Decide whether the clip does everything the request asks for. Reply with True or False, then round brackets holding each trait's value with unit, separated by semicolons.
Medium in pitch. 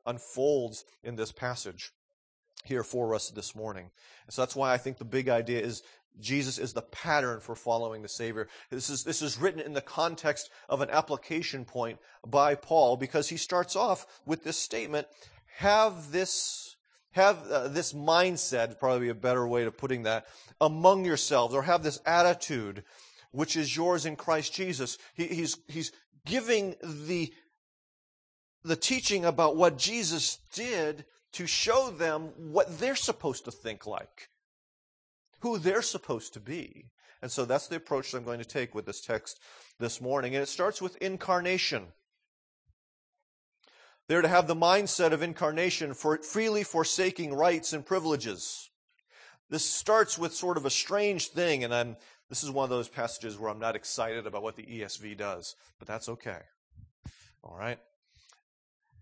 True (150 Hz)